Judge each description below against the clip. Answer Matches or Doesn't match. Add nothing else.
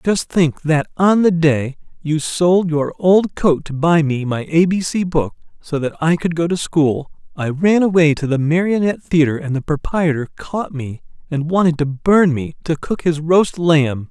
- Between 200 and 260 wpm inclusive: Matches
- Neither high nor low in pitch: Matches